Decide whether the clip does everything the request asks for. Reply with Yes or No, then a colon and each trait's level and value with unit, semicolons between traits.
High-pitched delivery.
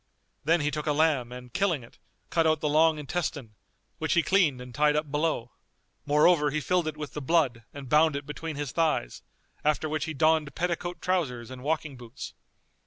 No: medium, 150 Hz